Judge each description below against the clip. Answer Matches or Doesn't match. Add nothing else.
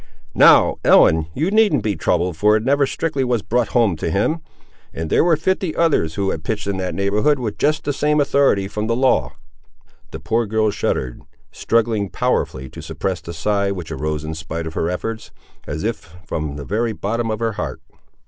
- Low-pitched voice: Matches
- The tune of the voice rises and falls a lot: Matches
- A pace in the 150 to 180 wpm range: Doesn't match